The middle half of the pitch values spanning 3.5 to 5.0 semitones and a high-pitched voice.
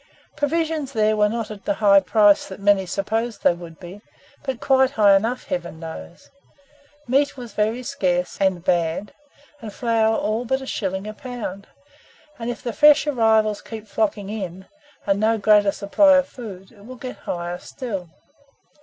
Yes: average, 3.8 semitones; high, 215 Hz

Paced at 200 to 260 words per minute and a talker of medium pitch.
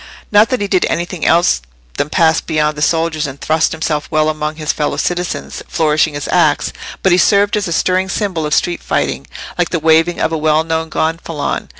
Yes: fast, 205 wpm; medium, 160 Hz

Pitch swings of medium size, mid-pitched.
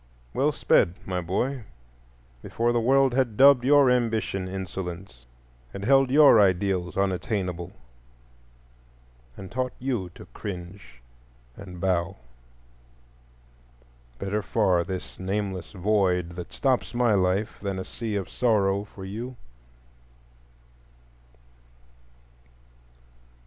No: average, 4.5 semitones; low, 100 Hz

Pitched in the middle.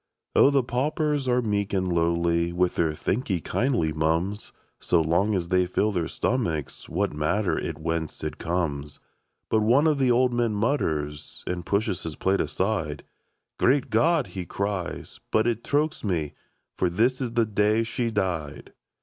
No: low, 100 Hz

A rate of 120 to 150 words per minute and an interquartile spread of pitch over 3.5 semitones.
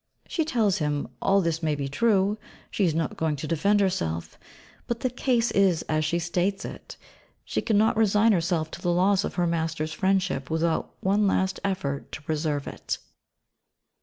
No: average, 175 wpm; average, 4.2 semitones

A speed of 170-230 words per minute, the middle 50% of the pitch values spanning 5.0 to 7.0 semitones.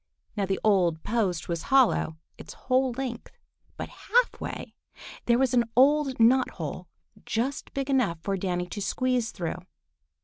No: average, 150 wpm; wide, 5.5 semitones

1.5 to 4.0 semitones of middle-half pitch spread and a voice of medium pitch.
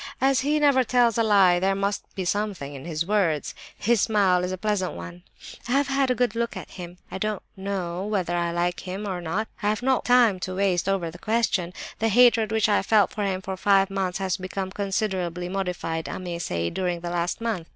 No: average, 3.4 semitones; high, 195 Hz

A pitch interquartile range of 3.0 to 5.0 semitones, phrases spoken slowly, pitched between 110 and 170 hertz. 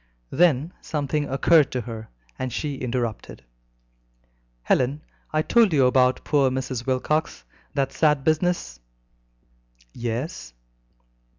Yes: average, 3.4 semitones; slow, 105 wpm; low, 135 Hz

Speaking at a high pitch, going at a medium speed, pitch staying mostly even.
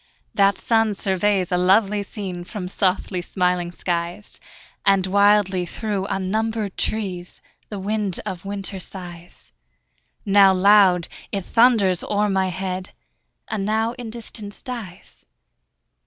No: high, 195 Hz; slow, 120 wpm; narrow, 2.3 semitones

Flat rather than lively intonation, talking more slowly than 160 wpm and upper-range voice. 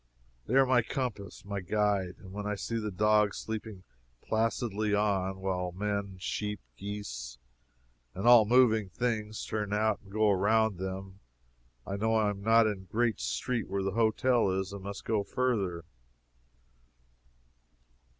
No: narrow, 2.3 semitones; average, 150 wpm; low, 105 Hz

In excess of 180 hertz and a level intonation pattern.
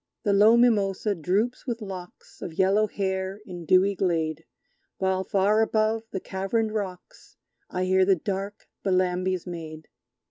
Yes: high, 190 Hz; narrow, 2.3 semitones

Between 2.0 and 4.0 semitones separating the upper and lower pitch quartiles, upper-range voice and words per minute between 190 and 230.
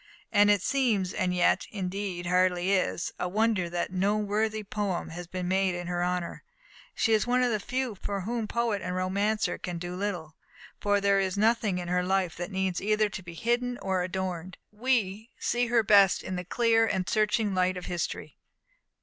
Yes: average, 3.0 semitones; high, 195 Hz; average, 195 wpm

